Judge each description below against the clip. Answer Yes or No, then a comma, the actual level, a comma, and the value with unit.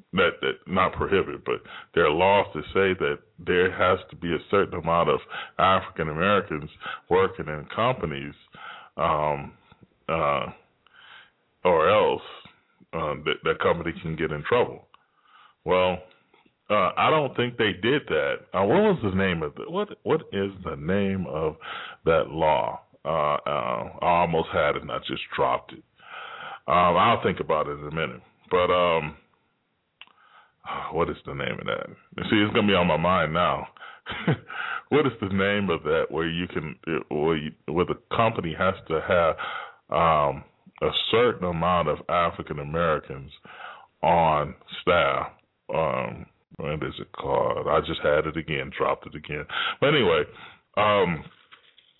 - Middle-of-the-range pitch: No, very low, 95 Hz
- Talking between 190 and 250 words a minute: No, average, 155 wpm